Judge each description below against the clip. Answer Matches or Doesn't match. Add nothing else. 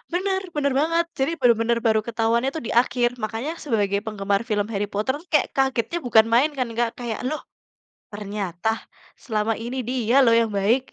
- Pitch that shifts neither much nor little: Matches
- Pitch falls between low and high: Doesn't match